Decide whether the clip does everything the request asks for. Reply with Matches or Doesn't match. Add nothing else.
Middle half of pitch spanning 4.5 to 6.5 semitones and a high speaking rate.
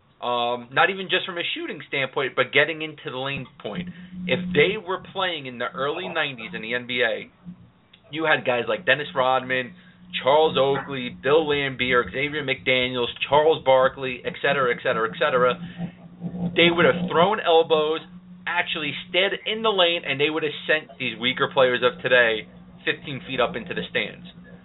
Doesn't match